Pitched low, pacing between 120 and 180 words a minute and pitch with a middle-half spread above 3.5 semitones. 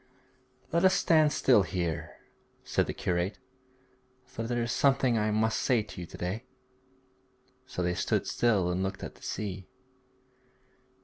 Yes: low, 110 Hz; average, 150 wpm; average, 5.1 semitones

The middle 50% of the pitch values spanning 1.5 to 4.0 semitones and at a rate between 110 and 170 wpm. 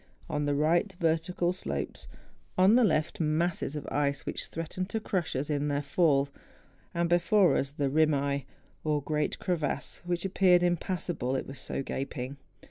Yes: average, 3.7 semitones; average, 160 wpm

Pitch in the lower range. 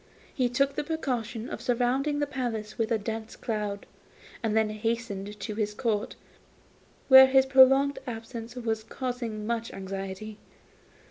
No: high, 230 Hz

